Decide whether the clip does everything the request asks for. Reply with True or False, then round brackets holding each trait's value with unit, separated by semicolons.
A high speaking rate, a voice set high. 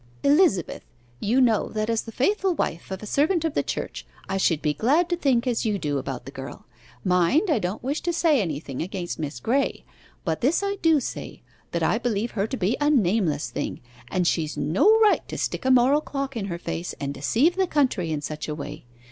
True (220 wpm; 220 Hz)